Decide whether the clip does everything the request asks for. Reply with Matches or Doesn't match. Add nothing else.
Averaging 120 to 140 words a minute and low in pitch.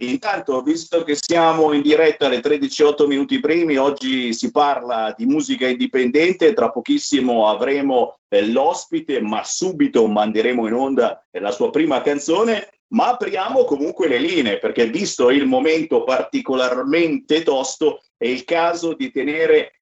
Doesn't match